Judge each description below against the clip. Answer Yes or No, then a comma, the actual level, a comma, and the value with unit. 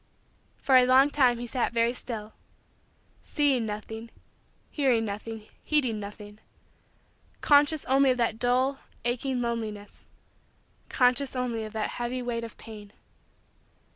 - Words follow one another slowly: Yes, slow, 125 wpm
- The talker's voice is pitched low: No, high, 240 Hz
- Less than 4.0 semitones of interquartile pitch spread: Yes, average, 2.7 semitones